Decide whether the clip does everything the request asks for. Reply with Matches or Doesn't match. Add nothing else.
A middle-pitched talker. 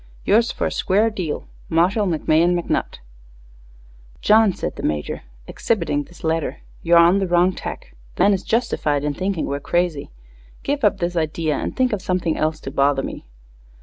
Matches